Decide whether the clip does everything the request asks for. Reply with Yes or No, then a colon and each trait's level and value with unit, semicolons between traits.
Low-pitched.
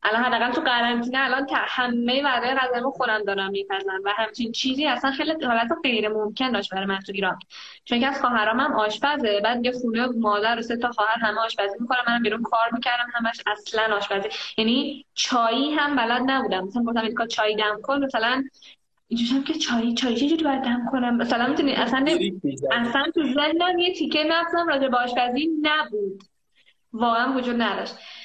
No: high, 240 Hz